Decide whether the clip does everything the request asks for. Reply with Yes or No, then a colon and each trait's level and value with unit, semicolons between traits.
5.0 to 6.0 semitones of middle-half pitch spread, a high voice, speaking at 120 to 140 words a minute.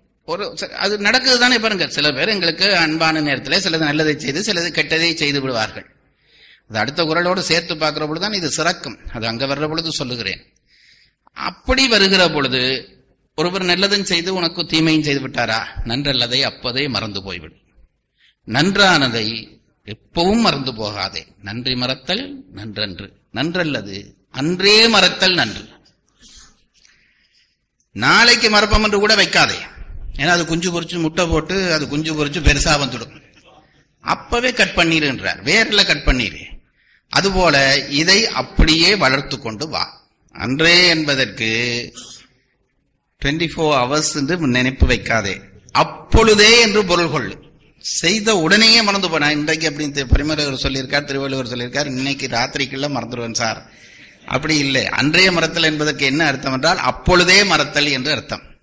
No: wide, 5.5 semitones; medium, 150 Hz; average, 125 wpm